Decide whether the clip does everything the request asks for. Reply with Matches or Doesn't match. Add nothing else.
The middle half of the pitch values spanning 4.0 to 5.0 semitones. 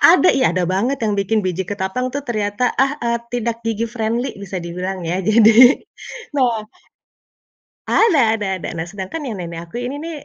Matches